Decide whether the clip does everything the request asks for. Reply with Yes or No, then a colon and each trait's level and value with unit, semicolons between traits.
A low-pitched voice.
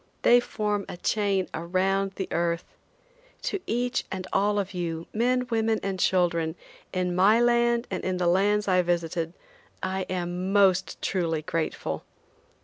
No: high, 190 Hz